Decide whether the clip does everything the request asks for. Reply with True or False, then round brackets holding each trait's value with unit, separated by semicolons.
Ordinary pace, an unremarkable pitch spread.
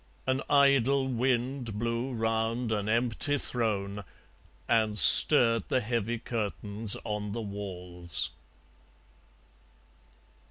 False (90 wpm; 3.0 semitones)